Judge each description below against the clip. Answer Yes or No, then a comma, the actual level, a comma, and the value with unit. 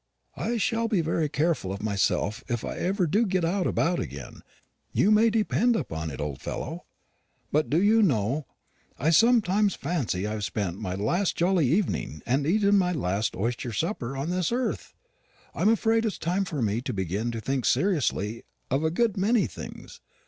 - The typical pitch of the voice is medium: Yes, medium, 160 Hz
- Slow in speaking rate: No, average, 180 wpm